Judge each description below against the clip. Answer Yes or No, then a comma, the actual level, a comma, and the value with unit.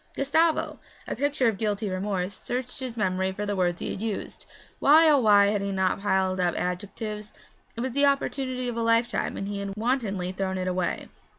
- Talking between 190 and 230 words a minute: Yes, average, 200 wpm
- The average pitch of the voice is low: No, high, 210 Hz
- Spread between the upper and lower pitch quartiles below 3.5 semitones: No, average, 4.7 semitones